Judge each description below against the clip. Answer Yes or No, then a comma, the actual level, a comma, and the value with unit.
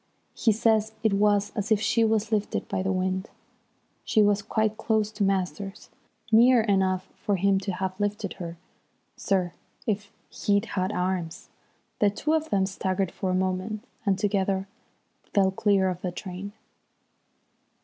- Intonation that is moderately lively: No, narrow, 2.1 semitones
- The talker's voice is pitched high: Yes, high, 200 Hz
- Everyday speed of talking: Yes, average, 155 wpm